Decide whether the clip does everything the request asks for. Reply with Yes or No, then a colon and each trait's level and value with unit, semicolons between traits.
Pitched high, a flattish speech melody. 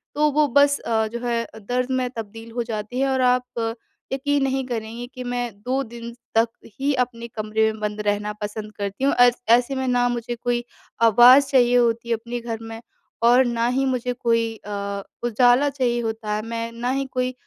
Yes: high, 240 Hz; narrow, 1.9 semitones